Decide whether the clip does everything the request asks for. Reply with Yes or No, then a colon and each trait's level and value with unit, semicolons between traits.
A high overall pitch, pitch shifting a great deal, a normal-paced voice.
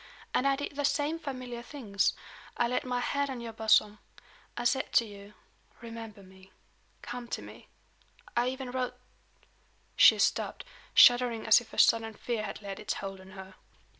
No: high, 235 Hz; average, 3.2 semitones; average, 175 wpm